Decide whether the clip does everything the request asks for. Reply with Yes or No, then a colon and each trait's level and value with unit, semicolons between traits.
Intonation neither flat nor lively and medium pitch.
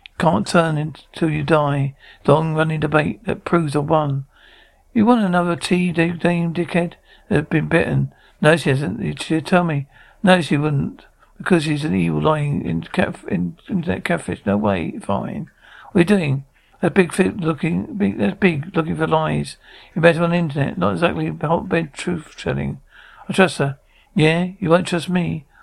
Yes: average, 3.3 semitones; medium, 160 Hz